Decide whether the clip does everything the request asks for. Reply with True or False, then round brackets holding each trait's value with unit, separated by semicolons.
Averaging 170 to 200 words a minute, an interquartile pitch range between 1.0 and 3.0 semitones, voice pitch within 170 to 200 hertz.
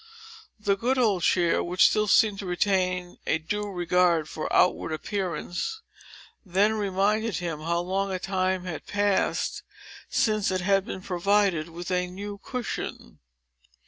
False (145 wpm; 2.5 semitones; 190 Hz)